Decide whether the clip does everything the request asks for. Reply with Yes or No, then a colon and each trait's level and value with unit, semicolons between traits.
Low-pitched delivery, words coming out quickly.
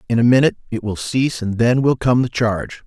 Yes: low, 120 Hz; fast, 250 wpm